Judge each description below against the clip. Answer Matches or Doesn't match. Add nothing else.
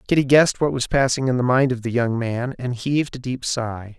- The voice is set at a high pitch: Doesn't match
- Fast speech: Matches